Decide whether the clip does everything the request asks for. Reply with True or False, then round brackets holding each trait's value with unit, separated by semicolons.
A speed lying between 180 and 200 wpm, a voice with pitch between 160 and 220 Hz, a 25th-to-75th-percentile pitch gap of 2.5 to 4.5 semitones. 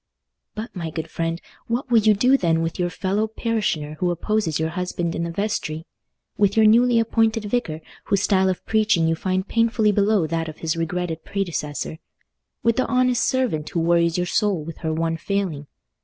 False (185 wpm; 185 Hz; 4.9 semitones)